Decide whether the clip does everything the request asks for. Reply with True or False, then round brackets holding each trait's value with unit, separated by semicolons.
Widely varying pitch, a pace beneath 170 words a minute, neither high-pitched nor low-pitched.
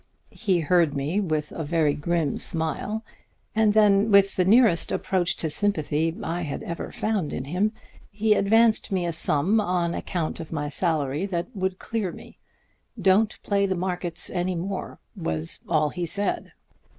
False (3.8 semitones; 160 wpm; 180 Hz)